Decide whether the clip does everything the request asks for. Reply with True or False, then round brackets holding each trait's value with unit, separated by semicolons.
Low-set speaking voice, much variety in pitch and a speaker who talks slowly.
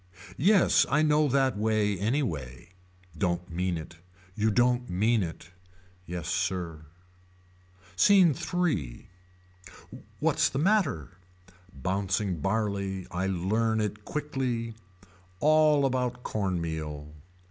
True (105 Hz; 6.6 semitones; 105 wpm)